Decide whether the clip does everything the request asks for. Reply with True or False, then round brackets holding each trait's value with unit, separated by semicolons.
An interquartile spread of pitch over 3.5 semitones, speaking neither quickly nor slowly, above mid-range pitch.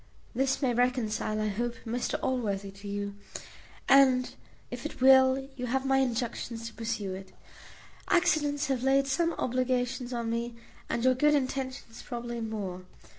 False (2.8 semitones; 150 wpm; 245 Hz)